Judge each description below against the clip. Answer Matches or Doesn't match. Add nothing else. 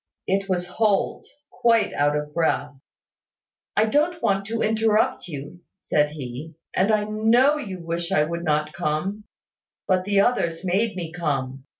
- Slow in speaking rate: Doesn't match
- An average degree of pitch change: Doesn't match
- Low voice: Doesn't match